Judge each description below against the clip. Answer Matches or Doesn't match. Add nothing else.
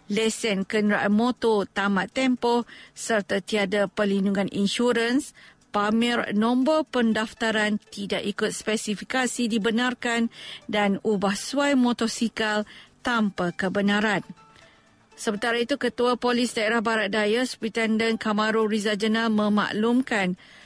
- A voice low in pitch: Doesn't match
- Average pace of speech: Matches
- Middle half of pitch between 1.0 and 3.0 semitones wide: Matches